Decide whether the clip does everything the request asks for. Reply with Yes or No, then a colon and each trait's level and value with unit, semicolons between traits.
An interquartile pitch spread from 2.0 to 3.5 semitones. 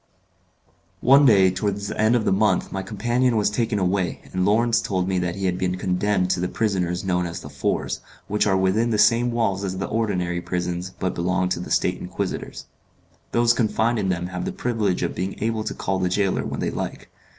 Yes: average, 3.2 semitones